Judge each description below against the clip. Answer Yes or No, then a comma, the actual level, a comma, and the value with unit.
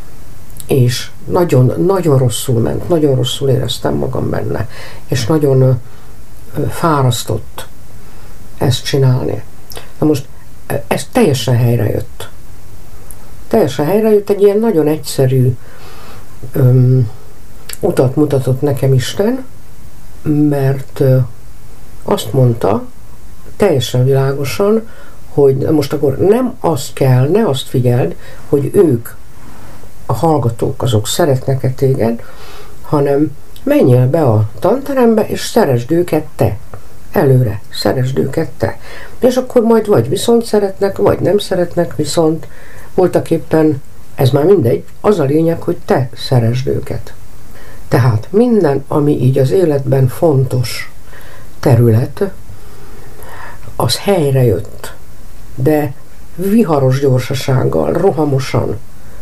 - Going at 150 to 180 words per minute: No, slow, 105 wpm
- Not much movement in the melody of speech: No, average, 4.7 semitones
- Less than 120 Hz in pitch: No, low, 130 Hz